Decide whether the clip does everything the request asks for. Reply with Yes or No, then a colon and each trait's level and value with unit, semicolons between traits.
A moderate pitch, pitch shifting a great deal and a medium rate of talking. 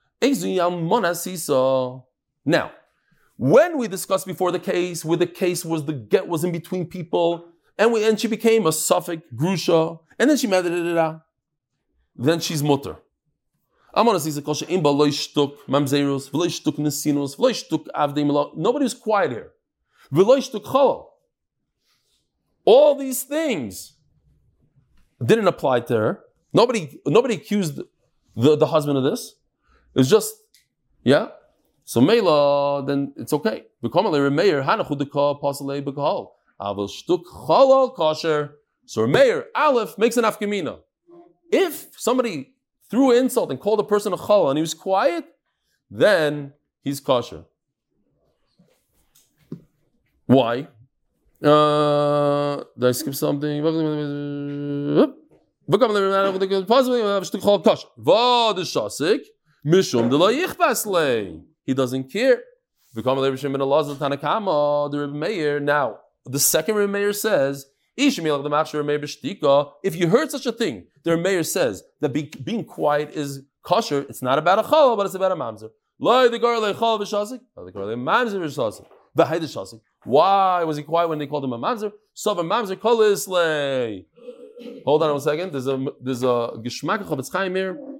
No: medium, 170 Hz; wide, 7.2 semitones; slow, 105 wpm